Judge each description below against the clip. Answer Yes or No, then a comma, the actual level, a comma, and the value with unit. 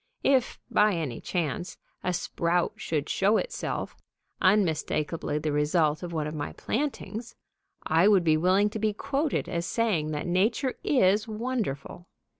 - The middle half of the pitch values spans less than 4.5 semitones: No, wide, 5.6 semitones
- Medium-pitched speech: Yes, medium, 180 Hz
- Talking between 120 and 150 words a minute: Yes, average, 145 wpm